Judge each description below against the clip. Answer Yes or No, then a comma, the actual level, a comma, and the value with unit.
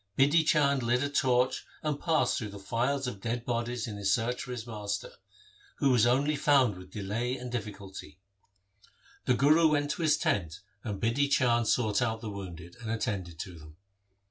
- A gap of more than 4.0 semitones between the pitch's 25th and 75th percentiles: Yes, average, 5.1 semitones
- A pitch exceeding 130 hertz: No, low, 120 Hz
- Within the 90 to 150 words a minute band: No, average, 180 wpm